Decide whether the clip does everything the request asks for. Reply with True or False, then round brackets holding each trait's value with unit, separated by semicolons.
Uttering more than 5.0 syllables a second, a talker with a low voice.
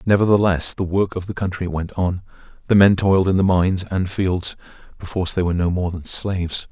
True (5.8 syllables/s; 90 Hz)